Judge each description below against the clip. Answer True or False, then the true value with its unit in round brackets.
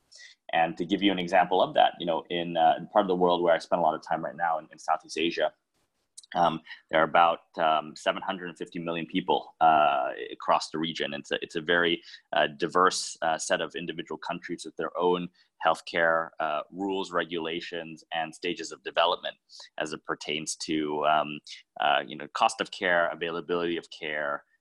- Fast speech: False (195 wpm)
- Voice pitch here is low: True (85 Hz)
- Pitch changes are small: True (1.6 semitones)